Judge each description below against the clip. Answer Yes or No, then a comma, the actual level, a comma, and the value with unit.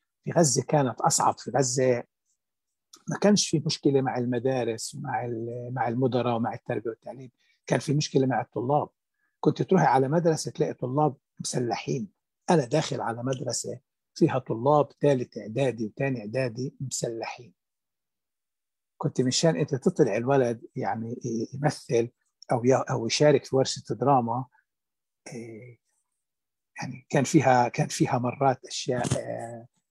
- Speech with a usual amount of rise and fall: Yes, average, 3.6 semitones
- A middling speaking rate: No, slow, 120 wpm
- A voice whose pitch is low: Yes, low, 130 Hz